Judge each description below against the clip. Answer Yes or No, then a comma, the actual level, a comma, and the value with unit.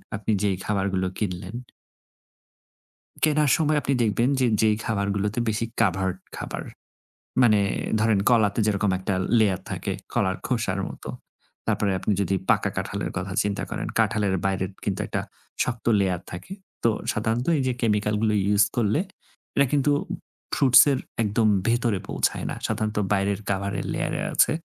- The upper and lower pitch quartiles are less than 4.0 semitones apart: Yes, average, 2.9 semitones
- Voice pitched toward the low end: Yes, low, 105 Hz